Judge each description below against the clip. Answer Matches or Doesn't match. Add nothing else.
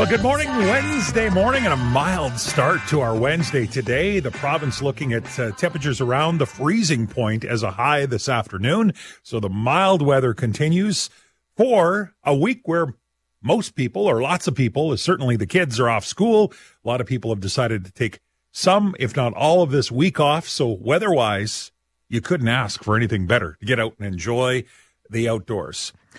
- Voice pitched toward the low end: Matches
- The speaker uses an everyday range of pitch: Doesn't match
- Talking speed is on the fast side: Doesn't match